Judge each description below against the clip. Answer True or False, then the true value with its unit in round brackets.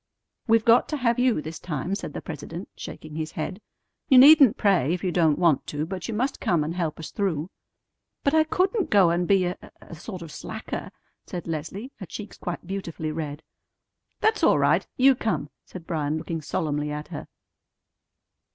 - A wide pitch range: True (5.8 semitones)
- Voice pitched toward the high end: False (175 Hz)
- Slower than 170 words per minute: False (190 wpm)